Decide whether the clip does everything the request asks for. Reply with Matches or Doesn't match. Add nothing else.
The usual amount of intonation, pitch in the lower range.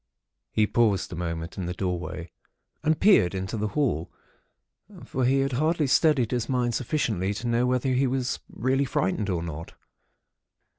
Doesn't match